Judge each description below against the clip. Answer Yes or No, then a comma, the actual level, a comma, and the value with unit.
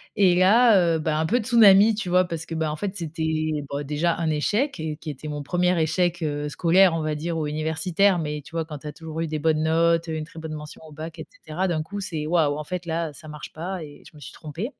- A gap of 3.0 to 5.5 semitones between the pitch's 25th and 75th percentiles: No, narrow, 2.6 semitones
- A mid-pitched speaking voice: Yes, medium, 160 Hz